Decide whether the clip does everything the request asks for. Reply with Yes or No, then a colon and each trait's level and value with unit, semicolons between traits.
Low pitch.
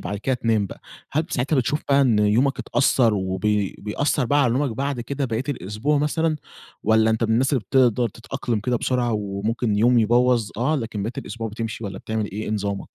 Yes: low, 115 Hz